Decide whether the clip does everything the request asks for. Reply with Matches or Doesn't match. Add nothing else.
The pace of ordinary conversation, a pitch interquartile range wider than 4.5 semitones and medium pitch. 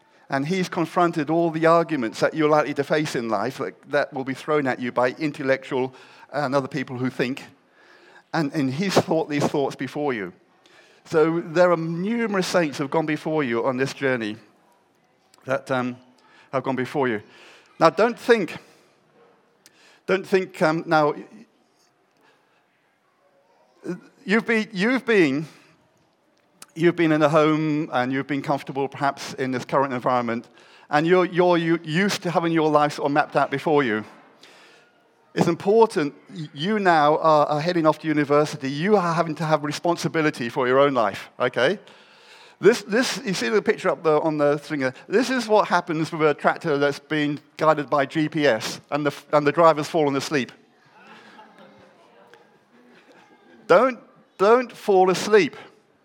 Doesn't match